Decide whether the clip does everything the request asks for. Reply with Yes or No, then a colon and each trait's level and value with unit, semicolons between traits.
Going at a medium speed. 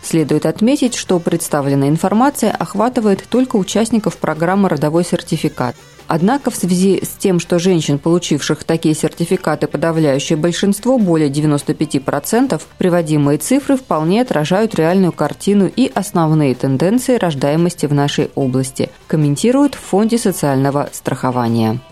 Yes: average, 120 wpm